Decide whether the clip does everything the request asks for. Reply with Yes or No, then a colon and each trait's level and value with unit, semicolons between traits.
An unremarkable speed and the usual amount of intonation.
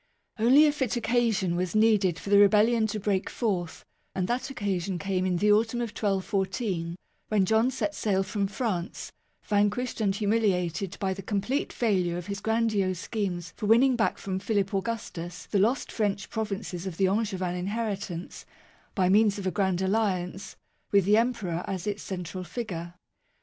Yes: average, 165 wpm; average, 3.0 semitones